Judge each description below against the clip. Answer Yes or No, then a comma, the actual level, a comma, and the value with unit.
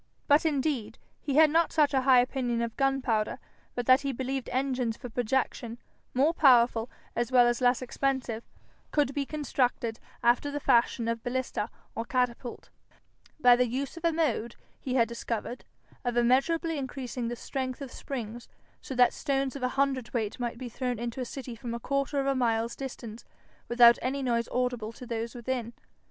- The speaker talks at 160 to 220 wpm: Yes, average, 175 wpm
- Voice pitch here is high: Yes, very high, 250 Hz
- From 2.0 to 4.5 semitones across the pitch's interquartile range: Yes, narrow, 2.4 semitones